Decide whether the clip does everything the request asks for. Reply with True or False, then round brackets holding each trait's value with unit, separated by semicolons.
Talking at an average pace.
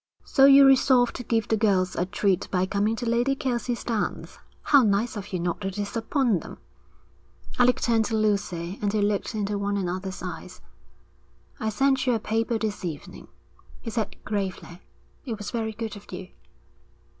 True (175 wpm)